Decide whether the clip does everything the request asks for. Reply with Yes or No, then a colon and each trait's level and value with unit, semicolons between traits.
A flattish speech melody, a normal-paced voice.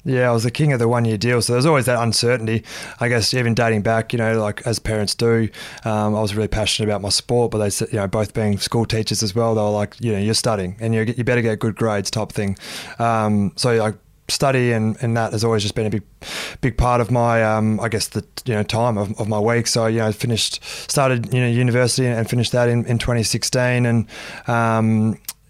No: narrow, 1.9 semitones; fast, 250 wpm